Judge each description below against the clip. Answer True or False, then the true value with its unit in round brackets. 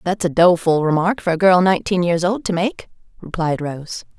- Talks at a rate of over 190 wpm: True (200 wpm)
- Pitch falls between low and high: True (175 Hz)